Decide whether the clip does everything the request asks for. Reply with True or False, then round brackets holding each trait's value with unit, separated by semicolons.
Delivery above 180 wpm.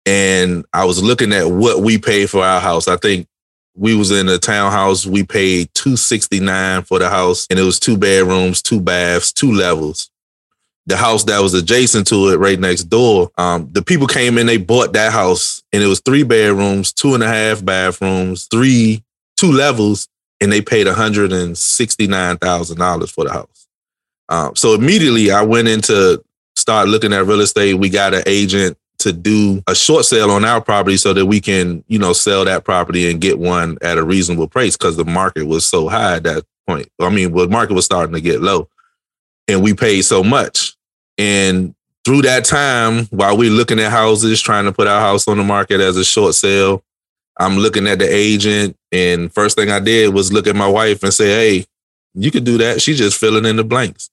True (205 wpm)